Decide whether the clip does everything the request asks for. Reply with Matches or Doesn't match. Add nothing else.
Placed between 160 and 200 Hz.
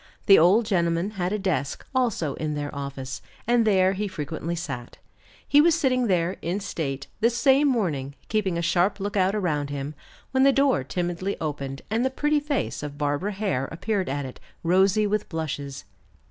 Matches